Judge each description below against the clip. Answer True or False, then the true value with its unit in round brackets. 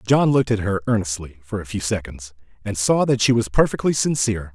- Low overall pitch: True (105 Hz)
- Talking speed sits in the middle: False (210 wpm)